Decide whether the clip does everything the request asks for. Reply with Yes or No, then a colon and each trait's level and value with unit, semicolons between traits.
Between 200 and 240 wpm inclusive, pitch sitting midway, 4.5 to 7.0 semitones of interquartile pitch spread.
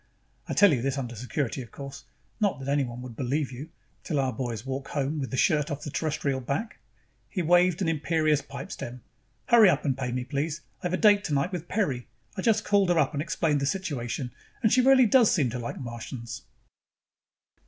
Yes: fast, 205 wpm; medium, 145 Hz; wide, 5.5 semitones